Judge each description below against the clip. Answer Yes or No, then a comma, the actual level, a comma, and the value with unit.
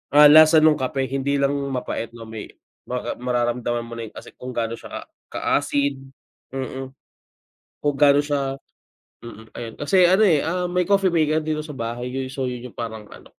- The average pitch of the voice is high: No, low, 135 Hz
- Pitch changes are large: No, average, 3.9 semitones